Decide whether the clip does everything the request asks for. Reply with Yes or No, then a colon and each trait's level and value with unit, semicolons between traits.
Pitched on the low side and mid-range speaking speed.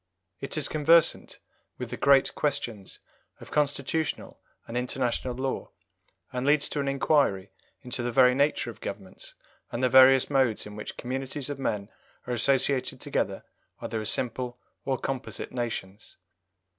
Yes: low, 130 Hz; average, 145 wpm